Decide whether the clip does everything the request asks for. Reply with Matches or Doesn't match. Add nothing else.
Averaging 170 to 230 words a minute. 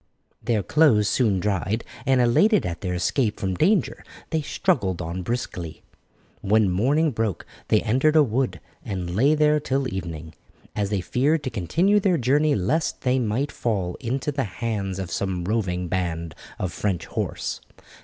Doesn't match